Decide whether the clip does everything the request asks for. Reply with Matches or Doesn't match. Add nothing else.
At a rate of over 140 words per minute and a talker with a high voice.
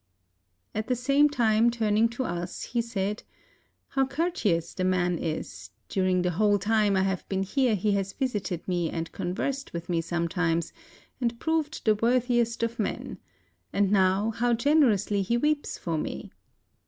Matches